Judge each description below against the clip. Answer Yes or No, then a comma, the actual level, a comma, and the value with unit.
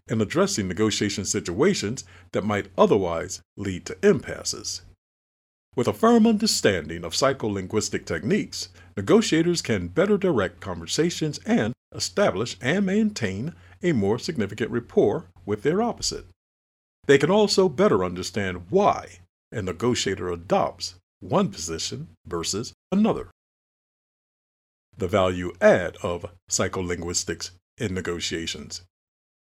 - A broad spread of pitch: Yes, wide, 5.9 semitones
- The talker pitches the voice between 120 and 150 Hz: No, very low, 95 Hz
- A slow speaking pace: Yes, slow, 110 wpm